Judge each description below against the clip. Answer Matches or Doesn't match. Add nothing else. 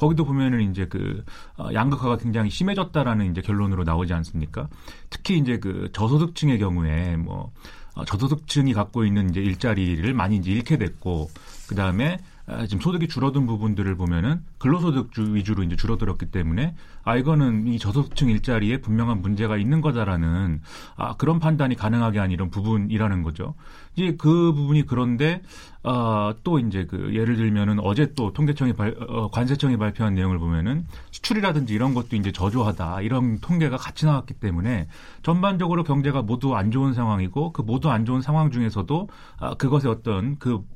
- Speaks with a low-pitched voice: Matches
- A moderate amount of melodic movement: Doesn't match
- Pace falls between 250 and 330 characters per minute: Doesn't match